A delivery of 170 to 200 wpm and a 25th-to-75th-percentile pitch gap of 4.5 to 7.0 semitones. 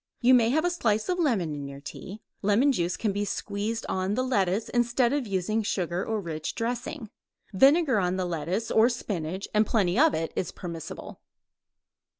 Yes: average, 180 wpm; average, 5.0 semitones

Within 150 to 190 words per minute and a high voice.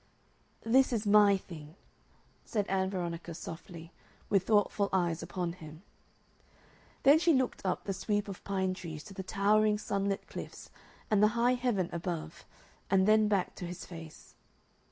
Yes: average, 155 wpm; high, 195 Hz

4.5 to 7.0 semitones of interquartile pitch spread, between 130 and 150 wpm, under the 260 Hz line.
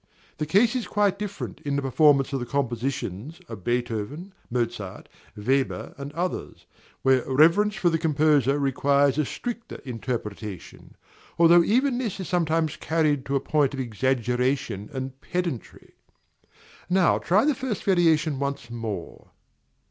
Yes: wide, 5.5 semitones; average, 140 wpm; medium, 140 Hz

